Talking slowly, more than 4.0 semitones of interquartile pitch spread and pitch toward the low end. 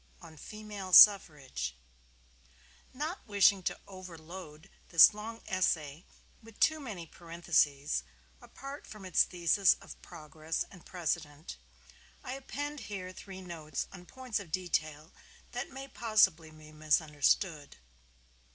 No: slow, 115 wpm; average, 5.2 semitones; medium, 180 Hz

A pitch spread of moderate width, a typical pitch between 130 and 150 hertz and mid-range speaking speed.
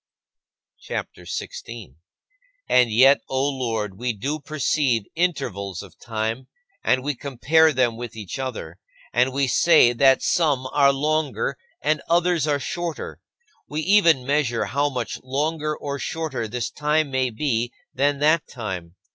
Yes: average, 4.2 semitones; low, 135 Hz; average, 145 wpm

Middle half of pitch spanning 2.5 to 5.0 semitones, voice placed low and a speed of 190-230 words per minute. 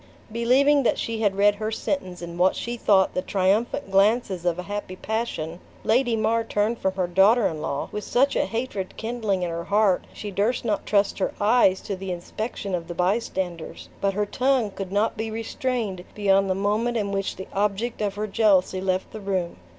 No: average, 3.1 semitones; high, 205 Hz; average, 200 wpm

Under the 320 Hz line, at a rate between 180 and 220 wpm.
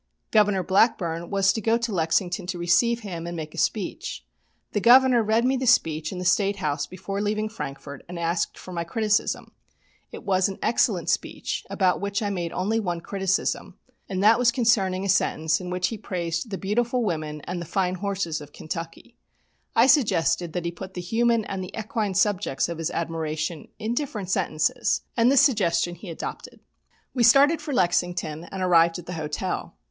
Yes: high, 190 Hz; average, 185 wpm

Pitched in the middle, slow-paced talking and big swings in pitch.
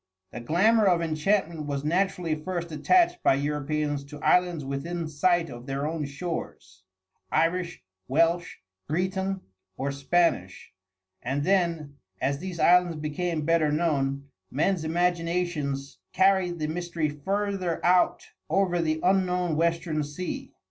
No: medium, 165 Hz; slow, 125 wpm; average, 3.4 semitones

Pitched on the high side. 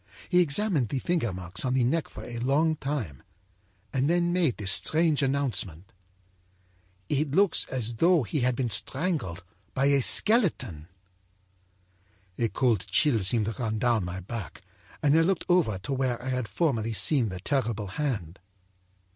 No: low, 130 Hz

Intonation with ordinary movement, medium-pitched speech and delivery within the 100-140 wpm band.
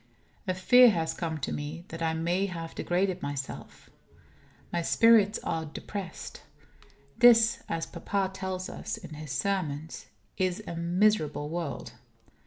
Yes: average, 3.5 semitones; medium, 175 Hz; slow, 135 wpm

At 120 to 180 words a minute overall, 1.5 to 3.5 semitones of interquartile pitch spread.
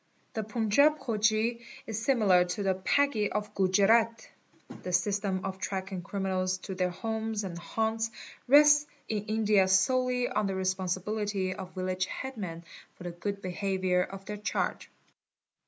Yes: average, 150 wpm; average, 2.9 semitones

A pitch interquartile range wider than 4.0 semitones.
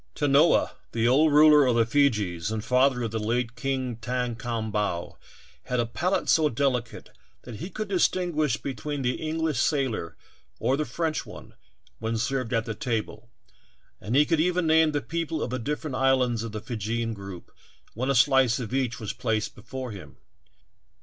Yes: average, 4.5 semitones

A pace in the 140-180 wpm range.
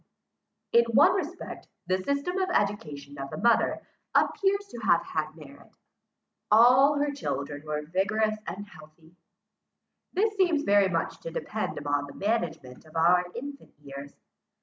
Yes: average, 145 wpm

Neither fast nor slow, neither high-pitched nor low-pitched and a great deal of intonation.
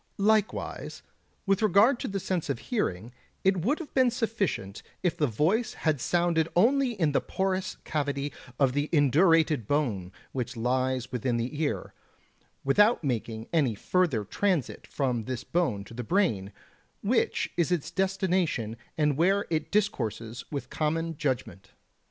Yes: average, 145 wpm; medium, 155 Hz; wide, 7.2 semitones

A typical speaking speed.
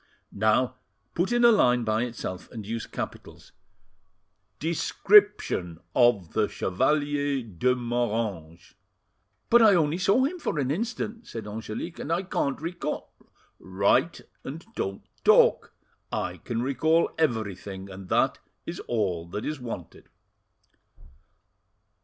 No: slow, 125 wpm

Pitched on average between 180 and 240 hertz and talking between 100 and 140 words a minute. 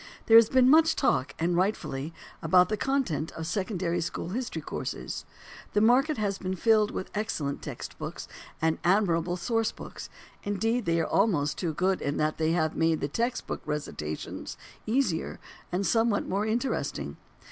No: high, 190 Hz; average, 160 wpm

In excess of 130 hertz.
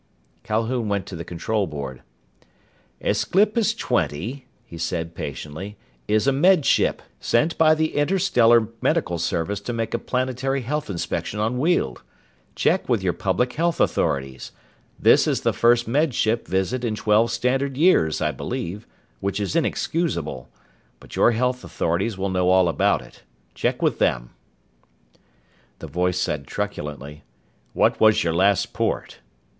No: low, 110 Hz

